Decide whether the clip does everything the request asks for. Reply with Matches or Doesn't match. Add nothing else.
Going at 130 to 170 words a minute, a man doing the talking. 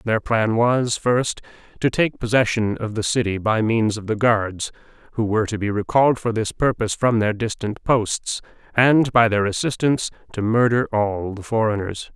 Doesn't match